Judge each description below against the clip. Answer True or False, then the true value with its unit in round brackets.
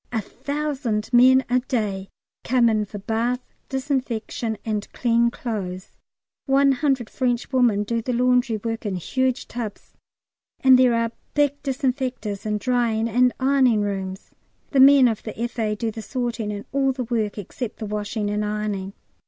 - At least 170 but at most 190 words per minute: False (155 wpm)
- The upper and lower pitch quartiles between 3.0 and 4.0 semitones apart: True (3.4 semitones)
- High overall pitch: True (235 Hz)